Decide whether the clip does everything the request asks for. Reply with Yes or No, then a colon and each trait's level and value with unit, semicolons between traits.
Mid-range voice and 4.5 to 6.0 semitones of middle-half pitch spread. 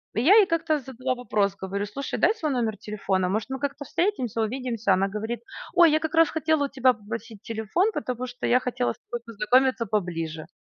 No: high, 240 Hz; average, 5.1 semitones